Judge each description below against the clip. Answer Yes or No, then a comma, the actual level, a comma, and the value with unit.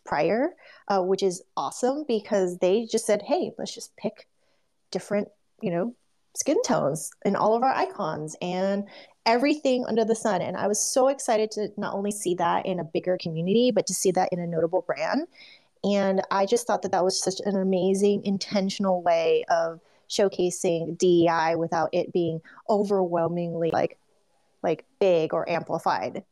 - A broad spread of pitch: No, average, 3.5 semitones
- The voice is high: Yes, high, 195 Hz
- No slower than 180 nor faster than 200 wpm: No, average, 170 wpm